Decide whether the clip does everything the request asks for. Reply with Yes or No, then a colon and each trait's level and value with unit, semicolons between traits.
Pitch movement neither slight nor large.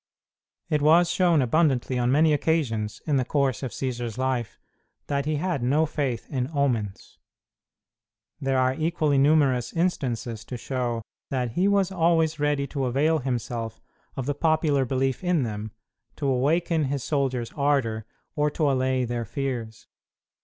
Yes: average, 3.9 semitones